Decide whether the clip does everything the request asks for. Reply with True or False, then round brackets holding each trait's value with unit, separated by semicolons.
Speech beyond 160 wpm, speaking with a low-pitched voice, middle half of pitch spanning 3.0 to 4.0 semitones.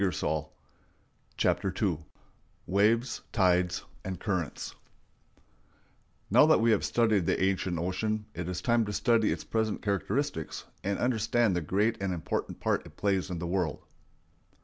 False (145 wpm; 100 Hz; 3.7 semitones)